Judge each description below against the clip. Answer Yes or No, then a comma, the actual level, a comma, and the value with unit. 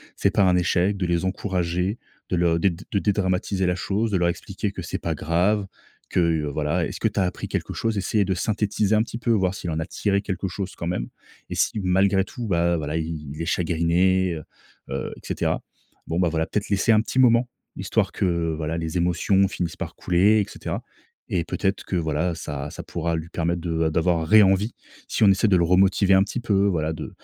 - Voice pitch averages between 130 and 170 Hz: No, very low, 90 Hz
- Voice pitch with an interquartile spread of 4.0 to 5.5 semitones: No, average, 3.0 semitones